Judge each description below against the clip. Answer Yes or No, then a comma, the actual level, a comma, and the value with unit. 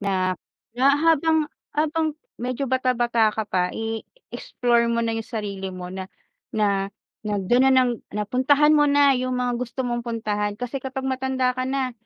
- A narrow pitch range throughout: No, average, 3.7 semitones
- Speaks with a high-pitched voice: Yes, high, 245 Hz